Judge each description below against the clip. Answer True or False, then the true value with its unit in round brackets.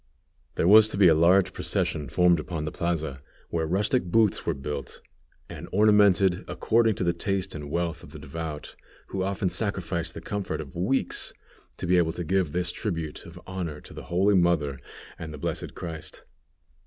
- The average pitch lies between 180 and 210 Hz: False (85 Hz)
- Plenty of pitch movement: False (3.3 semitones)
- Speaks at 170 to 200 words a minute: True (180 wpm)